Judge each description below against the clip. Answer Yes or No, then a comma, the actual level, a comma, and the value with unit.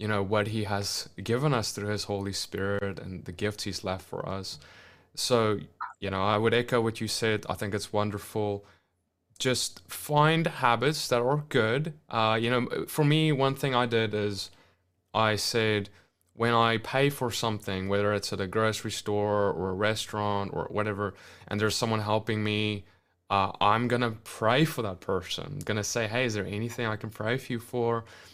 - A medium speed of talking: Yes, average, 195 wpm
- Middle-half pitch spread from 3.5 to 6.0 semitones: No, average, 2.9 semitones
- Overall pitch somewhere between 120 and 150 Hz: No, low, 105 Hz